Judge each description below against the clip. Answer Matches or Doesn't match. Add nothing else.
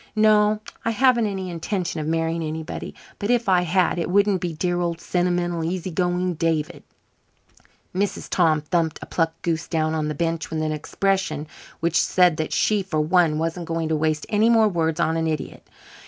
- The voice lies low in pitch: Doesn't match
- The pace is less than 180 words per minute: Doesn't match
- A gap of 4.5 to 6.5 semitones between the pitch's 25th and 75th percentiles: Doesn't match